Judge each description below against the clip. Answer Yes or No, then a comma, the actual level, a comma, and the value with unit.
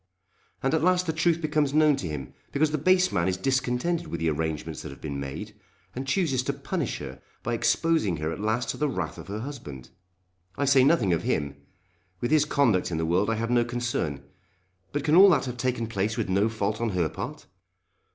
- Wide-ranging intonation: Yes, wide, 8.8 semitones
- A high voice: No, low, 120 Hz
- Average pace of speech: No, fast, 220 wpm